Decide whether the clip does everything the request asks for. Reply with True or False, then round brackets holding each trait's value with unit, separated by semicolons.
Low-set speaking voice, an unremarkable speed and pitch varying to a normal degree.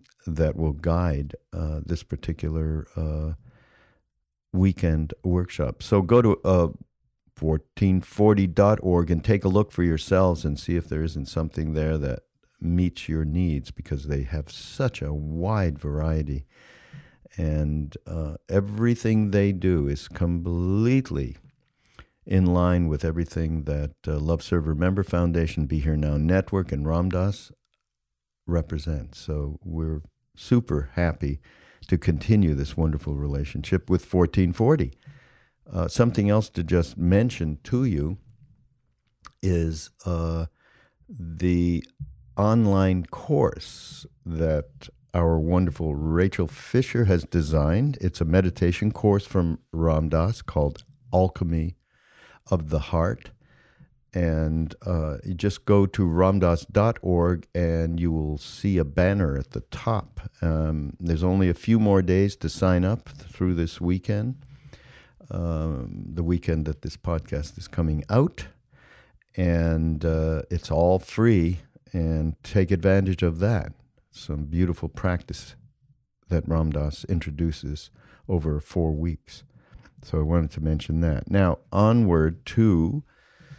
False (85 Hz; 125 wpm; 3.6 semitones)